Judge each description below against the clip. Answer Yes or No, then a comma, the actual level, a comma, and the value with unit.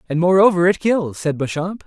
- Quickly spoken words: No, average, 195 wpm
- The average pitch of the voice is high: No, medium, 175 Hz